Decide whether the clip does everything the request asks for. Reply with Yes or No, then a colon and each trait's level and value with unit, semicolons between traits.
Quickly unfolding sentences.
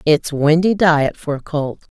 No: average, 180 wpm